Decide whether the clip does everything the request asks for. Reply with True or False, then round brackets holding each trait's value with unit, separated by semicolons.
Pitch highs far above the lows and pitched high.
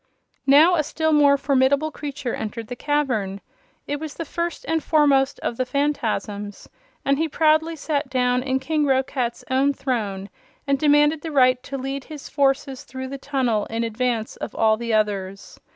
False (3.4 semitones; 270 Hz)